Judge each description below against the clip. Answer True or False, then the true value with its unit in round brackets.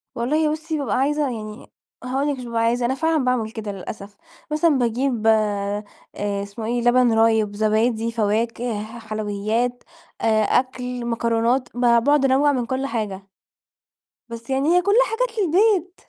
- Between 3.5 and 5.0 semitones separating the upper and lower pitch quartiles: True (3.8 semitones)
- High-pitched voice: True (240 Hz)